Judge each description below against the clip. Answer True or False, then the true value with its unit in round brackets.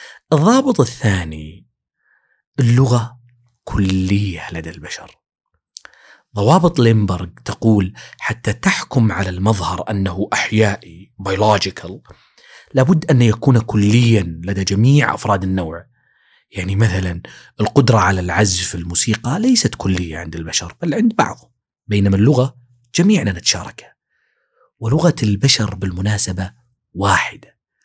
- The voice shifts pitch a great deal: False (4.6 semitones)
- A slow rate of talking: False (95 wpm)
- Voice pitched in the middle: False (105 Hz)